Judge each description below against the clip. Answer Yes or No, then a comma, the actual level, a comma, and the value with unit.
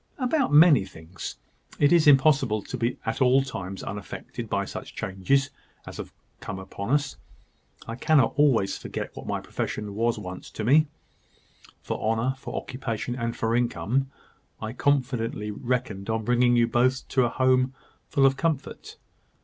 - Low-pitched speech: Yes, low, 120 Hz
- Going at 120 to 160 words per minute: Yes, average, 155 wpm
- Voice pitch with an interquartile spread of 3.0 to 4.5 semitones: Yes, average, 3.6 semitones